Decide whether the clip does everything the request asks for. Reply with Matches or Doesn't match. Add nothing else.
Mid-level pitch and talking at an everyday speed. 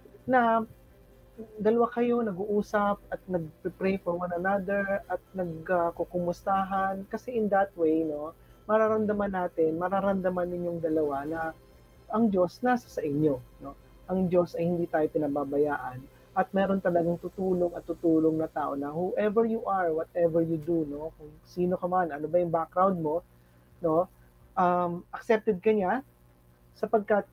Matches